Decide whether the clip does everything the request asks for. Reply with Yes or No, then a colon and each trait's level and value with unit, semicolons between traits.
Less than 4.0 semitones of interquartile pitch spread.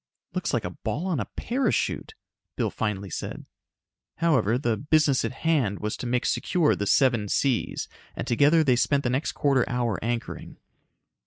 No: average, 4.7 semitones